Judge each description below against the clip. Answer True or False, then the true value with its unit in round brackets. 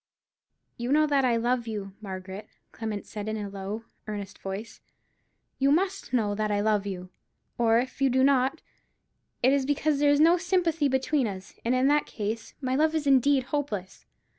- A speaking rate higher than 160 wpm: True (185 wpm)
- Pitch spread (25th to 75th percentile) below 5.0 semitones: False (5.4 semitones)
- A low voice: False (245 Hz)